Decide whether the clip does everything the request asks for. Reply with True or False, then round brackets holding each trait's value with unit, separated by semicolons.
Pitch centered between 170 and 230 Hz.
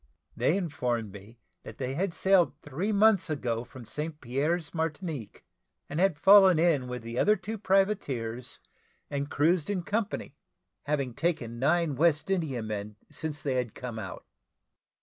False (145 Hz)